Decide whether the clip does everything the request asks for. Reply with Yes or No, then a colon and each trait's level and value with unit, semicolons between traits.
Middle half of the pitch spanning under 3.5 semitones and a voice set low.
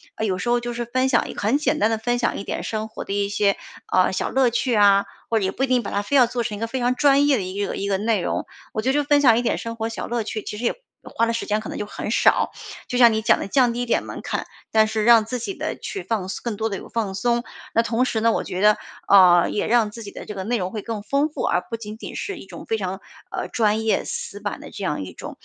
No: average, 2.9 semitones; high, 225 Hz